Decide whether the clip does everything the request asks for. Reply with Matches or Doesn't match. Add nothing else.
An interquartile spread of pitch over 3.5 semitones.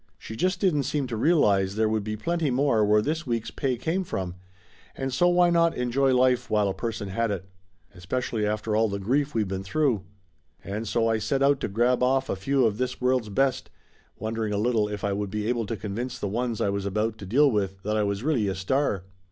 Matches